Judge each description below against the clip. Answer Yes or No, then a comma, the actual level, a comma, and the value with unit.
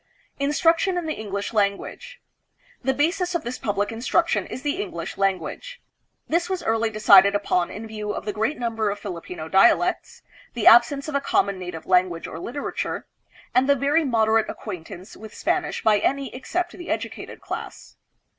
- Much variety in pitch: Yes, wide, 6.6 semitones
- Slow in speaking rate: No, average, 165 wpm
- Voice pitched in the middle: No, high, 225 Hz